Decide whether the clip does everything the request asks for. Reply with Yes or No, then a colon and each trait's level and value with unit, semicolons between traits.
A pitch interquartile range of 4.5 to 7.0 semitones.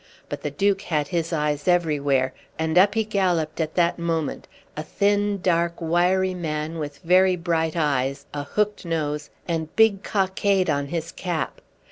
No: average, 3.5 semitones